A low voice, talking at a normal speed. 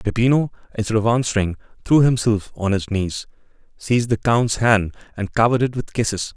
Yes: low, 110 Hz; average, 180 wpm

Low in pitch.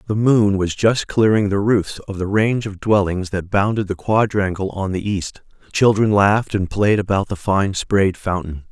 Yes: low, 100 Hz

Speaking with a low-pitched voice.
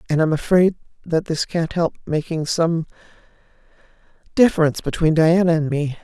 No: medium, 160 Hz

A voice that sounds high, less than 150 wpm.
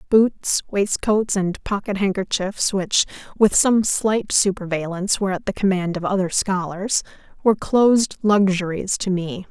Yes: high, 195 Hz; average, 140 wpm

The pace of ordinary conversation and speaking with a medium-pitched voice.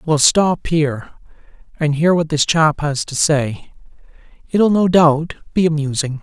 Yes: average, 155 wpm; medium, 155 Hz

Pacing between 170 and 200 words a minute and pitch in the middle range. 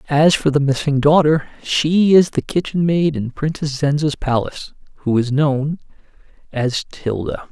No: average, 150 wpm; medium, 145 Hz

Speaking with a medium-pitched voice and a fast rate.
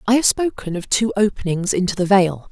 No: high, 200 Hz; fast, 215 wpm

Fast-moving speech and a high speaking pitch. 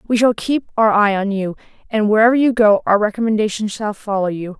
Yes: fast, 210 wpm; high, 215 Hz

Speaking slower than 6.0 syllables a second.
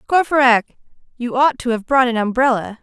Yes: 5.4 syllables/s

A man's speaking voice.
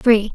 No: female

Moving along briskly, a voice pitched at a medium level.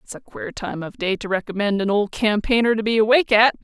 No: fast, 245 wpm; high, 215 Hz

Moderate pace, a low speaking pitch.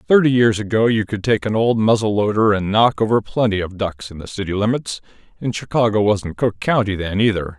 No: fast, 215 wpm; low, 105 Hz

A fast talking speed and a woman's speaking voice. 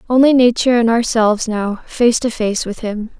No: average, 190 wpm; female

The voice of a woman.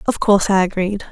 Yes: female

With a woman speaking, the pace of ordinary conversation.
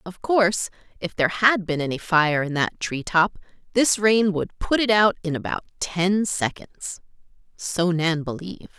Yes: female; average, 170 wpm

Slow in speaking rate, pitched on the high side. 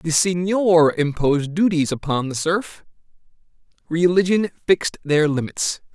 No: slow, 110 wpm; medium, 165 Hz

